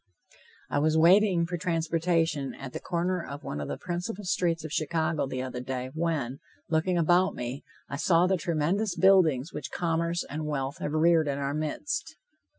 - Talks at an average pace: Yes, average, 175 wpm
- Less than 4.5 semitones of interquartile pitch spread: Yes, average, 3.4 semitones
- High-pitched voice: No, medium, 160 Hz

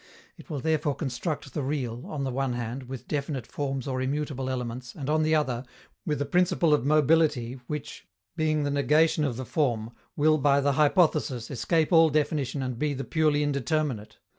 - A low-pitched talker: No, medium, 145 Hz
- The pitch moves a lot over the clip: No, average, 2.8 semitones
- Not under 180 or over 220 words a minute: Yes, average, 185 wpm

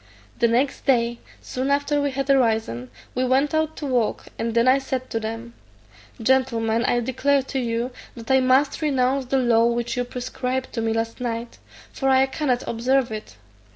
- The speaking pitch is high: Yes, very high, 255 Hz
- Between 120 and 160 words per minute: No, average, 185 wpm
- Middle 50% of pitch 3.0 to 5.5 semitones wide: No, narrow, 2.5 semitones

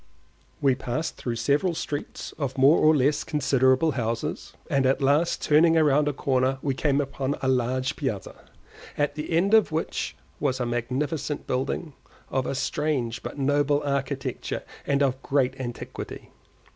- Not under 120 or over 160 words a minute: Yes, average, 155 wpm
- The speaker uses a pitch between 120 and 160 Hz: Yes, medium, 140 Hz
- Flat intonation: Yes, narrow, 2.2 semitones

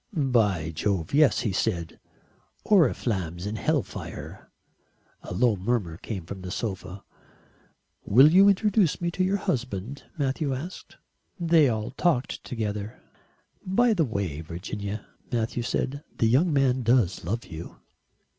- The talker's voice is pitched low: Yes, low, 115 Hz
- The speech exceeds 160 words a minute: No, slow, 135 wpm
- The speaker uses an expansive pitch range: Yes, wide, 7.1 semitones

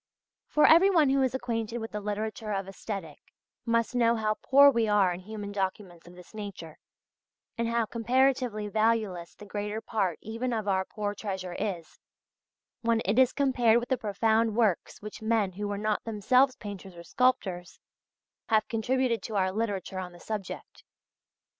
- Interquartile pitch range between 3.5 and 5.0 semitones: No, average, 2.9 semitones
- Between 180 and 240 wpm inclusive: No, average, 165 wpm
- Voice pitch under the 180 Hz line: No, high, 215 Hz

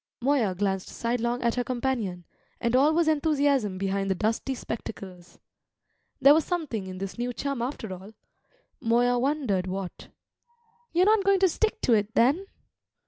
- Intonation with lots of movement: Yes, wide, 6.3 semitones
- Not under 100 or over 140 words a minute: No, average, 155 wpm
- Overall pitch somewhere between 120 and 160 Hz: No, high, 240 Hz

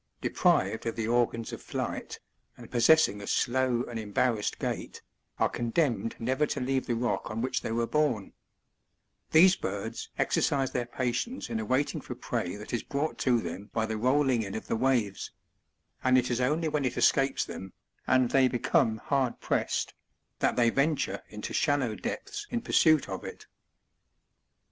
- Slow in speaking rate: No, average, 165 wpm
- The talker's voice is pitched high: No, low, 125 Hz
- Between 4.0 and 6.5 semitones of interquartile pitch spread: No, average, 3.4 semitones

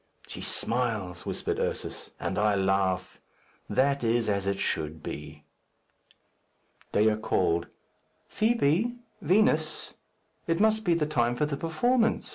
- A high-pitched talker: No, low, 120 Hz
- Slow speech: Yes, slow, 120 wpm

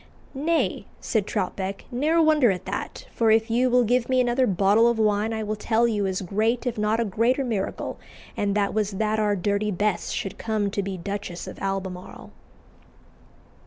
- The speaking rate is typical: Yes, average, 185 wpm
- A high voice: Yes, high, 215 Hz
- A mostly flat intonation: No, average, 3.1 semitones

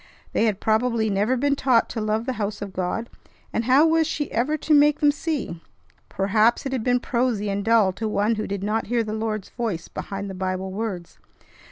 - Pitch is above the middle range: Yes, high, 220 Hz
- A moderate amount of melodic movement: Yes, average, 3.9 semitones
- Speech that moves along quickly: Yes, fast, 210 wpm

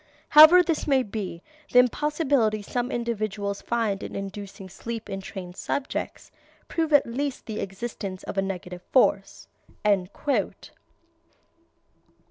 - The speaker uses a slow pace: Yes, slow, 115 wpm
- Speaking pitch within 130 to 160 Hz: No, high, 220 Hz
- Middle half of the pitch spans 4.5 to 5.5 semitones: Yes, average, 5.2 semitones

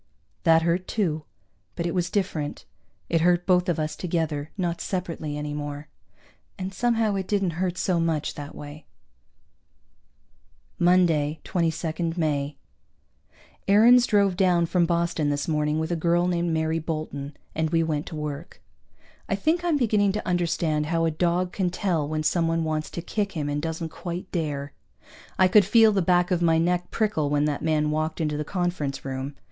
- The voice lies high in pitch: No, medium, 165 Hz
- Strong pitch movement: No, average, 2.9 semitones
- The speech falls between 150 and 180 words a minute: Yes, average, 175 wpm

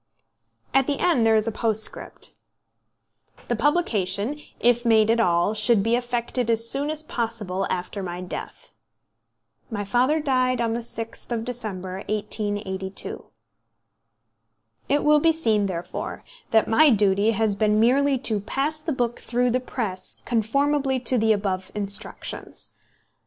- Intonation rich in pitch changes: No, average, 3.8 semitones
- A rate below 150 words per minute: Yes, average, 140 wpm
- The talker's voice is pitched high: Yes, high, 230 Hz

